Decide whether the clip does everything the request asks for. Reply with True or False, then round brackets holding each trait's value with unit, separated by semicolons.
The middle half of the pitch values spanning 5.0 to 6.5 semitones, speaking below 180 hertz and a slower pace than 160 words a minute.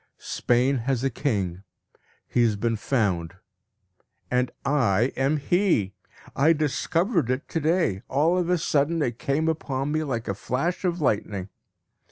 True (5.5 semitones; 135 Hz; 150 wpm)